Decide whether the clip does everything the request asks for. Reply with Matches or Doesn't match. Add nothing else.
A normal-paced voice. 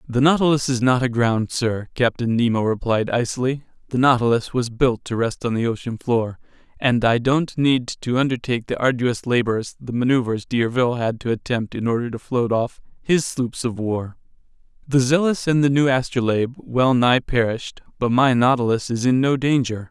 Matches